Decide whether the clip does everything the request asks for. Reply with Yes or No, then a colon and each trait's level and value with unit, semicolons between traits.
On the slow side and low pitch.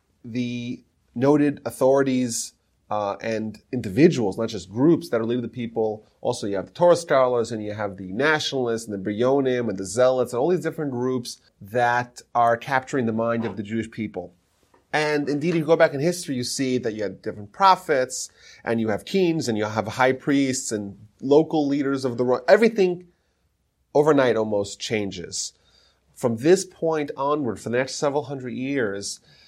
No: average, 180 wpm; low, 125 Hz